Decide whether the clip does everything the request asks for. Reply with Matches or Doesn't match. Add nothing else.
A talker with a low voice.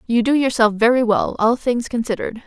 Doesn't match